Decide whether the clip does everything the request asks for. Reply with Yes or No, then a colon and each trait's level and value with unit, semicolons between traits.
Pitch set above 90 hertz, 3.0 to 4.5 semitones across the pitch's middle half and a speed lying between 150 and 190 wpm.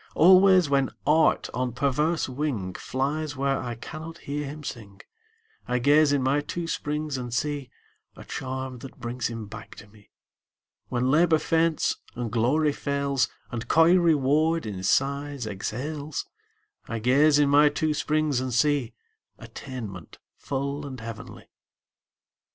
No: medium, 140 Hz; average, 3.6 semitones; average, 140 wpm